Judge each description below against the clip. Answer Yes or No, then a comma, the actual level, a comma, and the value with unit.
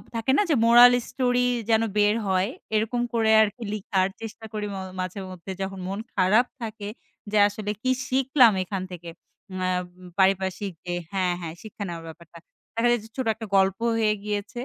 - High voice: Yes, high, 210 Hz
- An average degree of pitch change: Yes, average, 3.3 semitones